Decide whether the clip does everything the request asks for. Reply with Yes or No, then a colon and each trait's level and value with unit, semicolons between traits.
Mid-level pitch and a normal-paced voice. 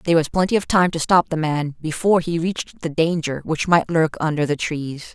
No: medium, 160 Hz; fast, 235 wpm